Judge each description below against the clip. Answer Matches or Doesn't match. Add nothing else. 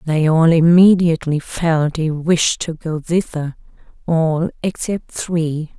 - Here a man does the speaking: Doesn't match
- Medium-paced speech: Doesn't match